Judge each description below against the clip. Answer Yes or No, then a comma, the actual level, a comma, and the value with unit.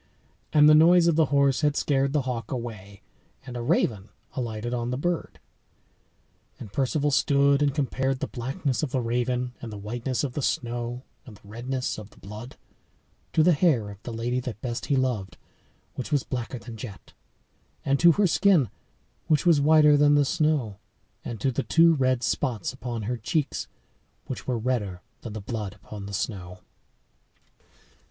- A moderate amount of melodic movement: Yes, average, 4.0 semitones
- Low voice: Yes, low, 125 Hz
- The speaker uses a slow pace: No, average, 175 wpm